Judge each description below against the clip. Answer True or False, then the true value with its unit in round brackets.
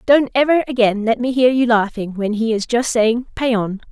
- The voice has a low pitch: False (235 Hz)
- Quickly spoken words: True (215 wpm)